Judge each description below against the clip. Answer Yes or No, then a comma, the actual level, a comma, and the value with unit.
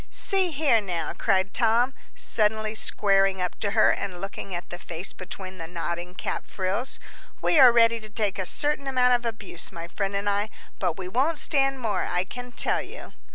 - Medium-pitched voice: No, high, 205 Hz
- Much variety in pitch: No, average, 4.7 semitones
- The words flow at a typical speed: Yes, average, 195 wpm